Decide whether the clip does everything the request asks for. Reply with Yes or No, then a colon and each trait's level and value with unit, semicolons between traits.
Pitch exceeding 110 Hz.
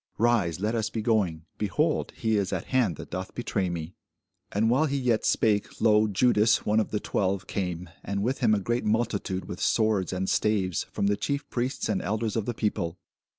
No: low, 105 Hz